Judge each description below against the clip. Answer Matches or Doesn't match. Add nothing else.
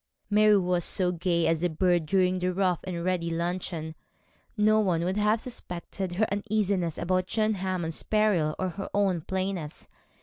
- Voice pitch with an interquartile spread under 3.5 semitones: Matches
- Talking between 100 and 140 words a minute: Doesn't match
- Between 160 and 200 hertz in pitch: Matches